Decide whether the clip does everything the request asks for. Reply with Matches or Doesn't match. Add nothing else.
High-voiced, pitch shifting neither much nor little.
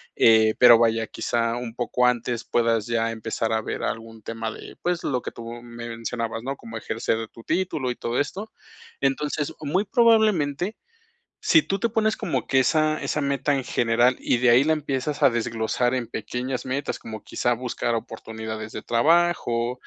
Doesn't match